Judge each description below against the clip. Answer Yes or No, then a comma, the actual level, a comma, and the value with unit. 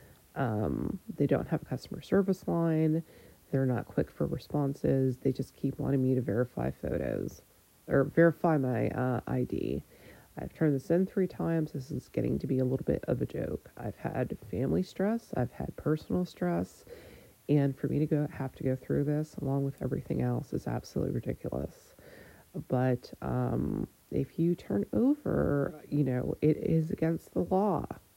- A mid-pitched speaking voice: Yes, medium, 145 Hz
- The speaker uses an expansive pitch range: No, average, 4.2 semitones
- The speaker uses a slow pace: No, average, 175 wpm